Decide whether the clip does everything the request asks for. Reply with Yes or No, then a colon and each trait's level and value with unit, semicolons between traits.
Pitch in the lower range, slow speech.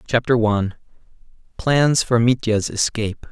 Yes: low, 120 Hz; slow, 110 wpm